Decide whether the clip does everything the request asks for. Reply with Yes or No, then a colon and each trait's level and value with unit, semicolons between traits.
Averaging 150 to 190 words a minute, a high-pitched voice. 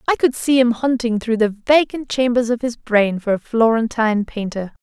No: average, 200 wpm; high, 235 Hz